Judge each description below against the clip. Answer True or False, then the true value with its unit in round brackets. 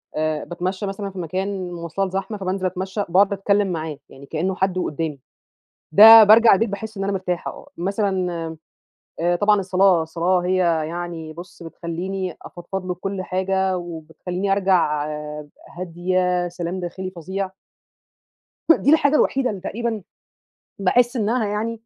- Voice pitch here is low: False (185 Hz)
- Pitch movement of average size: False (2.3 semitones)